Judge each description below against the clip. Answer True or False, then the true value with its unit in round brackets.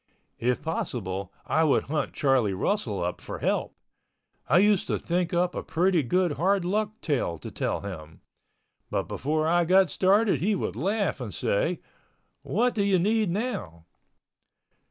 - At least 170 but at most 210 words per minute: False (155 wpm)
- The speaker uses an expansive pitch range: True (8.0 semitones)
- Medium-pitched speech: True (175 Hz)